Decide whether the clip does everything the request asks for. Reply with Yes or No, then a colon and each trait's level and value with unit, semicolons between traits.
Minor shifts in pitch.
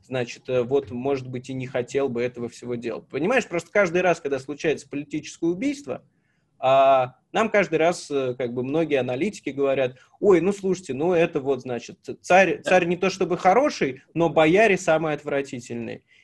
No: wide, 5.4 semitones